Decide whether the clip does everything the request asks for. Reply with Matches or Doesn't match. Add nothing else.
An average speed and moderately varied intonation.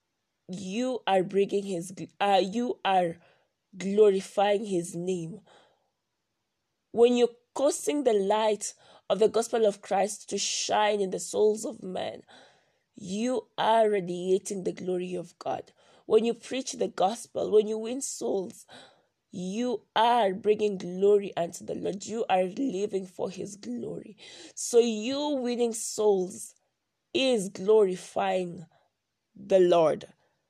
Doesn't match